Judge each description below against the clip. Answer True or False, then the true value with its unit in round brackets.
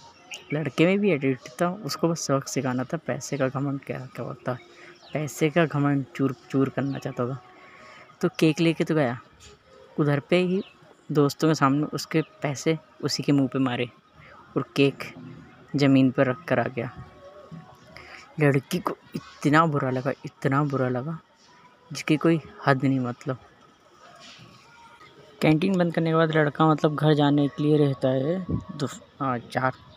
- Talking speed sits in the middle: True (150 wpm)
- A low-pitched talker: False (145 Hz)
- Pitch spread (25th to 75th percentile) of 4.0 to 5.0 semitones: False (3.3 semitones)